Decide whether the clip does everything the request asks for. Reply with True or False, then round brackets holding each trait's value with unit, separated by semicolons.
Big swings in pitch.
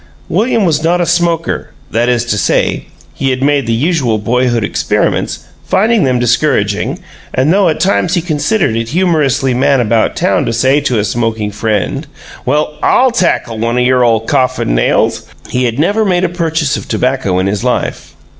True (6.4 semitones)